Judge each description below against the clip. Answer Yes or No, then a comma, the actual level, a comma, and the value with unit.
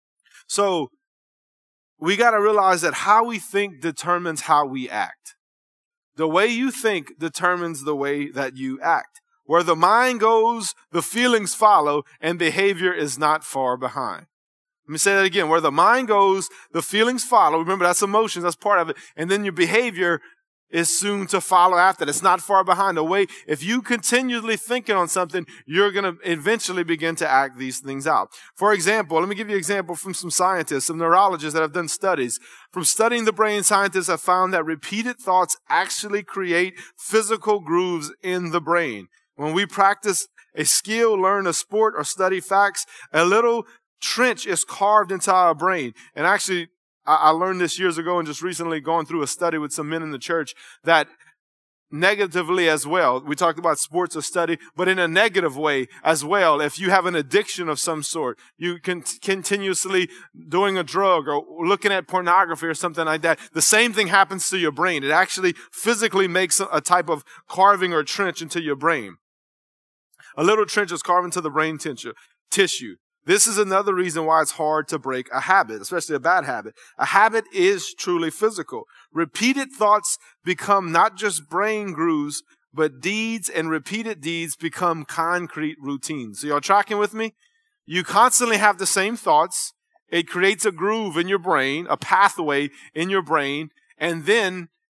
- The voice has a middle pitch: Yes, medium, 180 Hz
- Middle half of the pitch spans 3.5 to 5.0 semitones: Yes, average, 4.1 semitones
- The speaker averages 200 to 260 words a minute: No, average, 180 wpm